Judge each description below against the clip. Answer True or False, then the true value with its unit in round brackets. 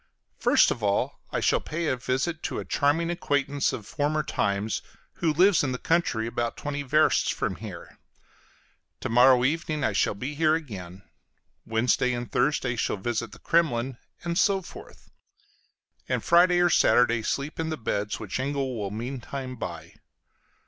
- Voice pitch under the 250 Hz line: True (135 Hz)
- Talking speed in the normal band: True (165 wpm)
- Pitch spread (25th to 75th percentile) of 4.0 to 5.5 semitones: True (5.0 semitones)